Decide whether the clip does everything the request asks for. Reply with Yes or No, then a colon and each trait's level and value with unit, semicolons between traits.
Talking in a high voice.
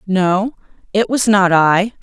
Yes: high, 200 Hz